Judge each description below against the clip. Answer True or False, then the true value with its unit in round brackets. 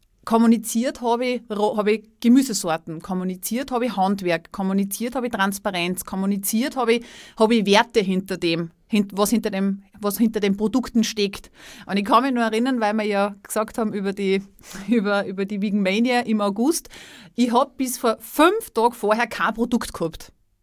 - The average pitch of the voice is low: False (215 Hz)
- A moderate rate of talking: True (170 wpm)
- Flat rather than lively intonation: False (3.3 semitones)